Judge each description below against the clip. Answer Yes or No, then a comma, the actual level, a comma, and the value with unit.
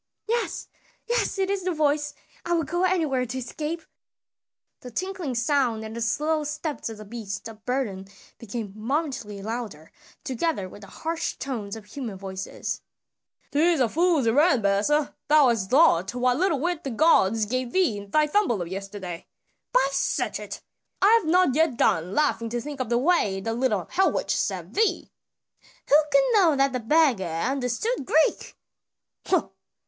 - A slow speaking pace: No, average, 165 wpm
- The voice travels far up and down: Yes, wide, 6.5 semitones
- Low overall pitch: No, very high, 260 Hz